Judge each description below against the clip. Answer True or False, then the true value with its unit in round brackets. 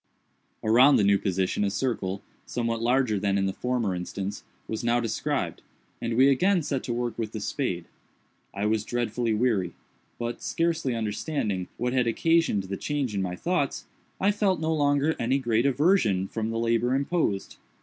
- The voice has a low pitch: True (120 Hz)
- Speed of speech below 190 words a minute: True (170 wpm)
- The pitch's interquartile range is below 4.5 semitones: False (5.1 semitones)